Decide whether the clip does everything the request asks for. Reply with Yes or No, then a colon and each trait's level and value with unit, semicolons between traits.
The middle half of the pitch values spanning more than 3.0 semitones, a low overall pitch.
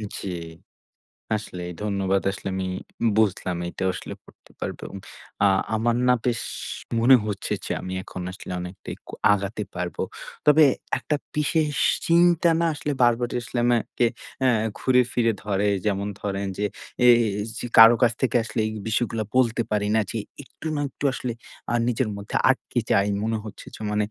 Yes: average, 3.7 semitones; low, 110 Hz